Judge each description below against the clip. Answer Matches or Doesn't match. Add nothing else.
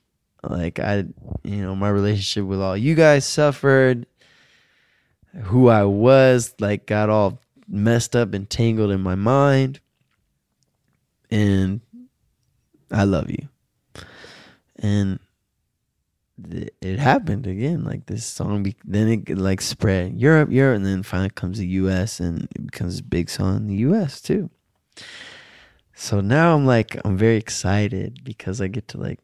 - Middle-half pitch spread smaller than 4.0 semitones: Doesn't match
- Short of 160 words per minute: Matches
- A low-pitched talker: Matches